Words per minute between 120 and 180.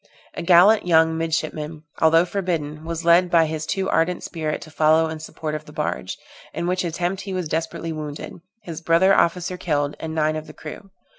No: average, 195 wpm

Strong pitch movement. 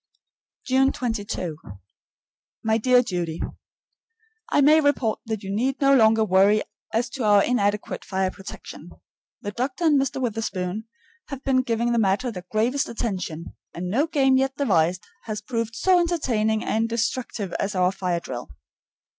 No: average, 4.9 semitones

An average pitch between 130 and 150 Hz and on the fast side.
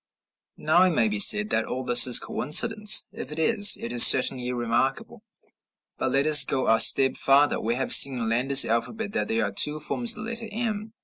Yes: low, 135 Hz; fast, 210 wpm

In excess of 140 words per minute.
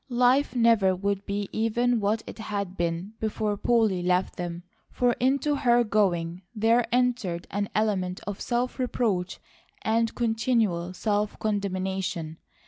No: slow, 135 wpm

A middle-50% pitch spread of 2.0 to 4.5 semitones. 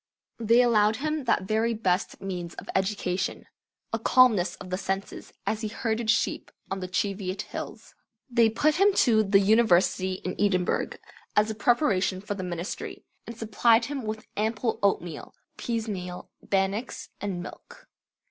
Yes: average, 3.5 semitones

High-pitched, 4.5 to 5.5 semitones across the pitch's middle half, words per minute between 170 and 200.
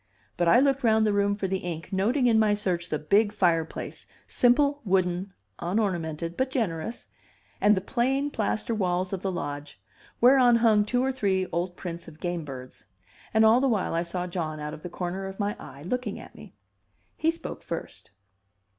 Yes: high, 195 Hz; average, 4.9 semitones; average, 185 wpm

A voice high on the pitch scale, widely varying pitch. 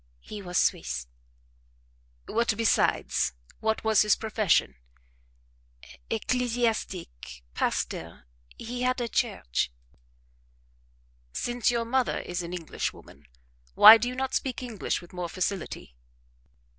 Yes: high, 215 Hz; wide, 5.9 semitones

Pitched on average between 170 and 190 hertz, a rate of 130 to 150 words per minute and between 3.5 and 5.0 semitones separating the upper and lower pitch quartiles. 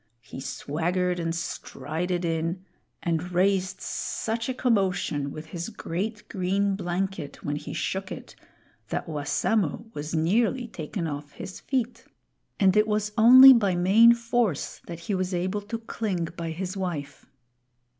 Yes: medium, 185 Hz; average, 145 wpm; average, 4.2 semitones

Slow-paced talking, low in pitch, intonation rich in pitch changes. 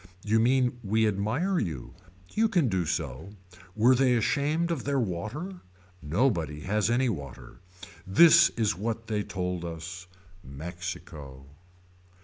Yes: slow, 130 wpm; low, 105 Hz; wide, 7.2 semitones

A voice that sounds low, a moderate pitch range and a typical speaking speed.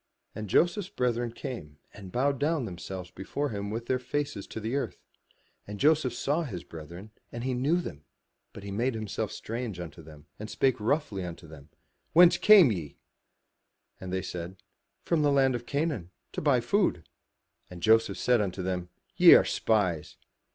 No: low, 110 Hz; wide, 6.8 semitones; average, 170 wpm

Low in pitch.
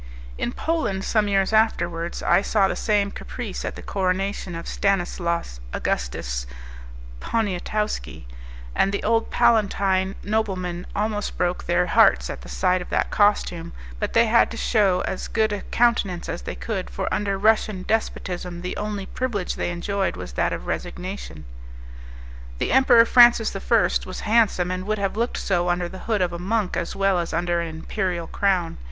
No: high, 195 Hz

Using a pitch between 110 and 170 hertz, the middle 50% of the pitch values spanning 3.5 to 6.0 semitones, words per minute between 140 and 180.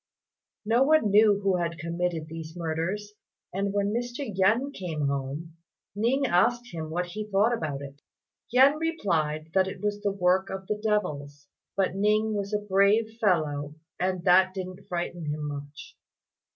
No: high, 190 Hz; average, 4.5 semitones; average, 155 wpm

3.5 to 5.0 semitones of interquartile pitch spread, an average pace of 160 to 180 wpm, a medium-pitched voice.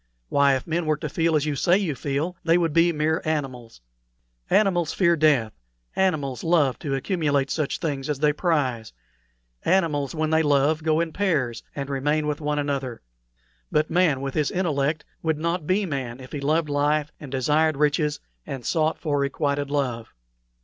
No: narrow, 2.6 semitones; average, 175 wpm; medium, 150 Hz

